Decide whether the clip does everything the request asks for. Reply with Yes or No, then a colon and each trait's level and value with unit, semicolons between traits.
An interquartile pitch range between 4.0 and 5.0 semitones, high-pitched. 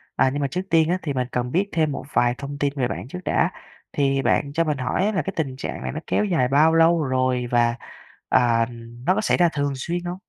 No: average, 4.6 semitones; medium, 145 Hz